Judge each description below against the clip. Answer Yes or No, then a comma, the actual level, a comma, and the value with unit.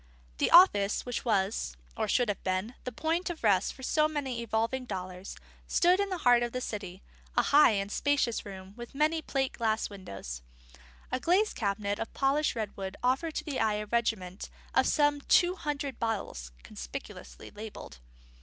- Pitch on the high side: Yes, high, 235 Hz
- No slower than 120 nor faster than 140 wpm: No, average, 175 wpm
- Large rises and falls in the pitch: Yes, wide, 6.4 semitones